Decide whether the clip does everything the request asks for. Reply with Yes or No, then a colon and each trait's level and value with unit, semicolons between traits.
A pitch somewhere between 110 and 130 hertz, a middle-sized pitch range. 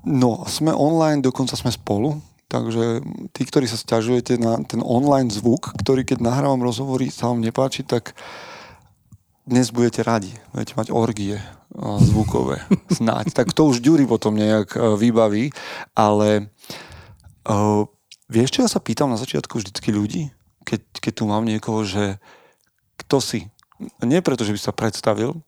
Yes: low, 115 Hz; average, 3.5 semitones